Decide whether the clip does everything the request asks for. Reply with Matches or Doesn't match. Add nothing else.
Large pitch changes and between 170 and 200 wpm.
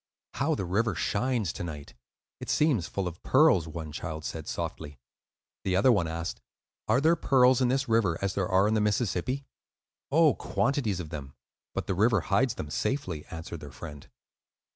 Matches